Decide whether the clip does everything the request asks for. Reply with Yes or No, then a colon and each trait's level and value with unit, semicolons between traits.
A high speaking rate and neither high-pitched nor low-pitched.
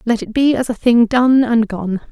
No: fast, 255 wpm; high, 235 Hz